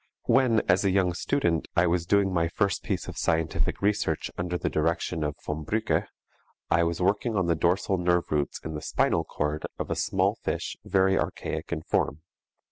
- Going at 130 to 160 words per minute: No, average, 190 wpm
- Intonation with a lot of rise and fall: No, average, 3.0 semitones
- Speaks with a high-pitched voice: No, very low, 90 Hz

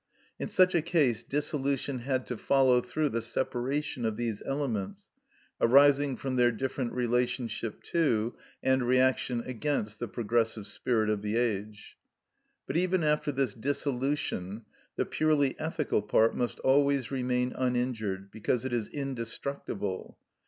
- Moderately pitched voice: No, low, 125 Hz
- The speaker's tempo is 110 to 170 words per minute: Yes, slow, 135 wpm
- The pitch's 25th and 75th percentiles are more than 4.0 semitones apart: No, average, 3.4 semitones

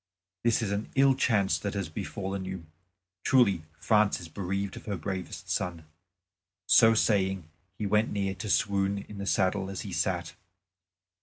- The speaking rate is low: No, average, 160 wpm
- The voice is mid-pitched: No, low, 100 Hz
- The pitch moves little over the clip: Yes, narrow, 1.9 semitones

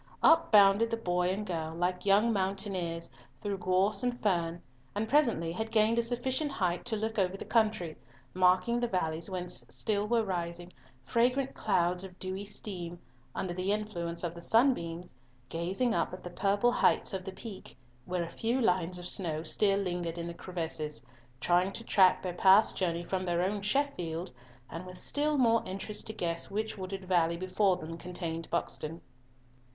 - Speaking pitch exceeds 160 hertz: Yes, medium, 185 Hz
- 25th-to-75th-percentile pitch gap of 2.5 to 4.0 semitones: Yes, average, 3.7 semitones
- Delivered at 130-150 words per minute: No, average, 175 wpm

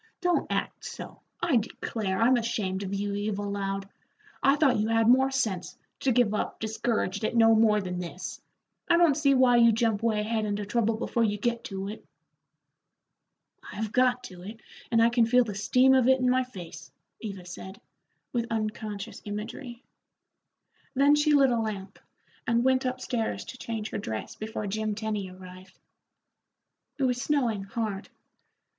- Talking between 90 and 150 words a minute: No, average, 170 wpm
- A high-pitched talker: Yes, high, 225 Hz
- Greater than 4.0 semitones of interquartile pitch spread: No, average, 3.5 semitones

